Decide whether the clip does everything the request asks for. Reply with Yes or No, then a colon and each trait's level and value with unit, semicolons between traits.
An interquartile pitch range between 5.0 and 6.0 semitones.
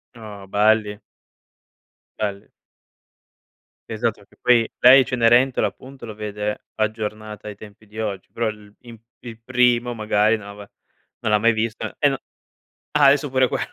No: narrow, 2.4 semitones